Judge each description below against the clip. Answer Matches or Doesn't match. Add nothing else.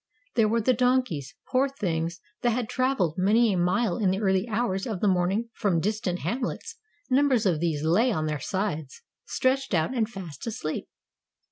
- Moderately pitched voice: Doesn't match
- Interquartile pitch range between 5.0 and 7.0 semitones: Matches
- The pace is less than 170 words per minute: Doesn't match